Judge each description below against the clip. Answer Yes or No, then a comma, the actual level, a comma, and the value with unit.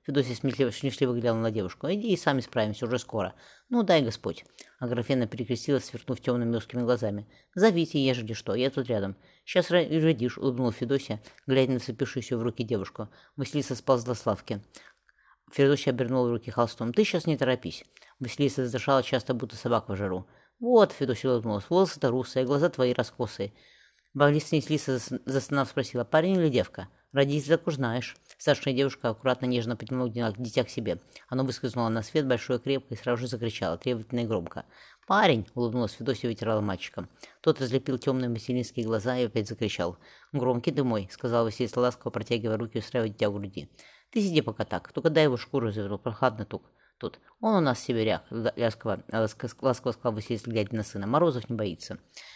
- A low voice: Yes, low, 125 Hz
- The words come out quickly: Yes, fast, 170 wpm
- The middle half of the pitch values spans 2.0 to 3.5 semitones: Yes, average, 3.2 semitones